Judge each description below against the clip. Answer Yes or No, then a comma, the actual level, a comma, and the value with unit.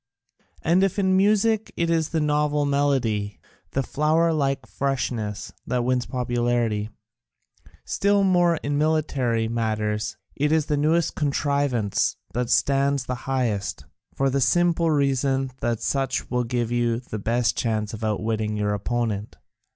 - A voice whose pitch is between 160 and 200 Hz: No, low, 135 Hz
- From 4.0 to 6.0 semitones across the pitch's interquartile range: Yes, average, 4.6 semitones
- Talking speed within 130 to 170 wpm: Yes, average, 140 wpm